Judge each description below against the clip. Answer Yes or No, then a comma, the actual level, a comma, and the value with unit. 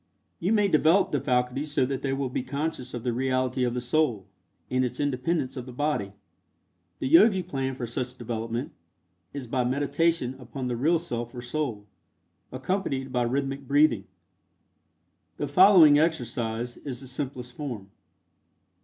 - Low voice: Yes, low, 130 Hz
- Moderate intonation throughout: Yes, average, 3.1 semitones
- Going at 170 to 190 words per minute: No, average, 155 wpm